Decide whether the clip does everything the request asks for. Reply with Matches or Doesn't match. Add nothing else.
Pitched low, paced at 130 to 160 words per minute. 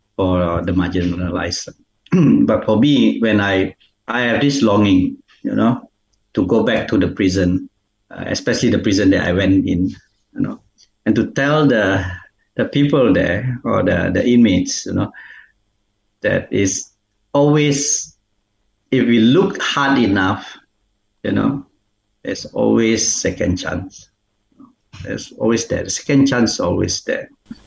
Matches